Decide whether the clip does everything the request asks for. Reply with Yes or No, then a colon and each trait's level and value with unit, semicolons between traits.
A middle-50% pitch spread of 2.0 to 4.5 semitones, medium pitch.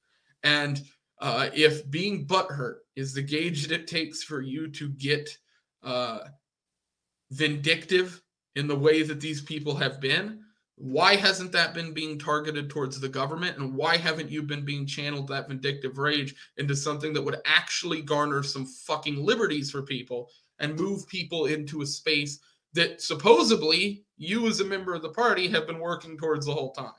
Yes: average, 3.1 semitones; medium, 150 Hz